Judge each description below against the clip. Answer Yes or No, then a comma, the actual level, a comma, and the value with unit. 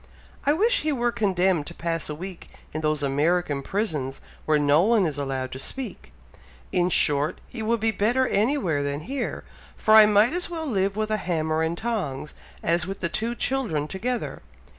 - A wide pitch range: Yes, wide, 7.1 semitones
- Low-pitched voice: No, medium, 185 Hz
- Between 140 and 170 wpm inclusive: No, average, 185 wpm